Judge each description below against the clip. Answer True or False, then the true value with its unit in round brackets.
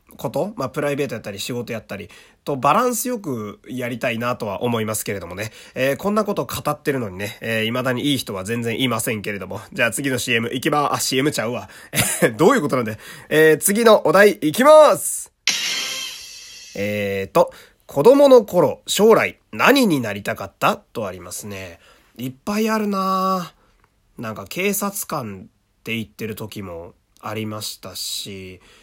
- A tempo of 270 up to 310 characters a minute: False (345 characters per minute)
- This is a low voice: True (125 Hz)